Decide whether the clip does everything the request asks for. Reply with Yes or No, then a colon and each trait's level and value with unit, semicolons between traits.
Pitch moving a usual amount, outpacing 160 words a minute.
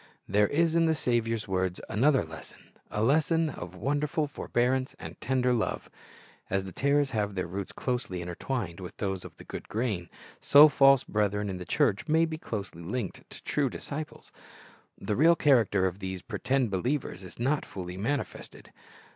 No: wide, 6.8 semitones; average, 170 wpm